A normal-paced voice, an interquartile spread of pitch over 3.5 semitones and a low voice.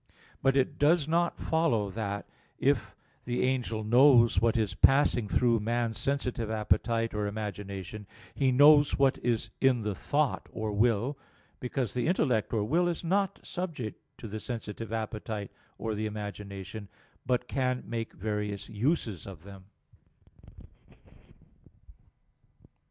No: slow, 130 wpm; average, 4.2 semitones; low, 115 Hz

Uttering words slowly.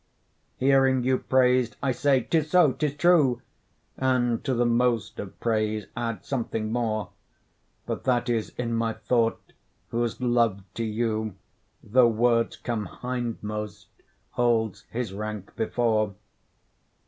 Yes: slow, 125 wpm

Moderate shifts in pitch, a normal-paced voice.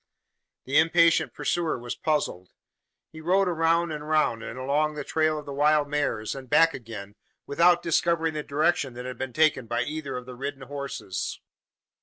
Yes: average, 3.6 semitones; average, 175 wpm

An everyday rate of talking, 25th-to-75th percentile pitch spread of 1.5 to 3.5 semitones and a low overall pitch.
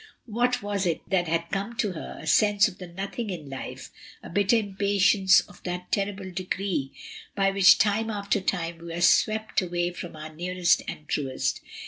No: average, 180 wpm; average, 2.9 semitones; high, 190 Hz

